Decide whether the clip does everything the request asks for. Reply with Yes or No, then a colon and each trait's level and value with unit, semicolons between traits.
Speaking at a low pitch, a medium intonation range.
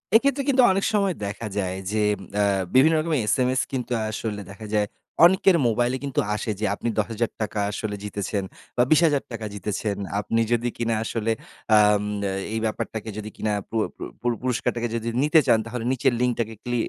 Yes: low, 115 Hz; average, 3.5 semitones